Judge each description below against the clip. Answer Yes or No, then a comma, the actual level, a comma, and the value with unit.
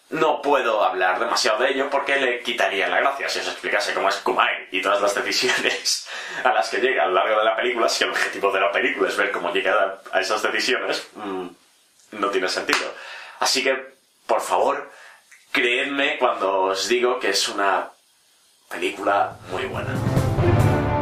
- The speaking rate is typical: Yes, average, 175 wpm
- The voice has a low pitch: Yes, low, 125 Hz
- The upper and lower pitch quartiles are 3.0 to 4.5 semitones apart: No, average, 5.0 semitones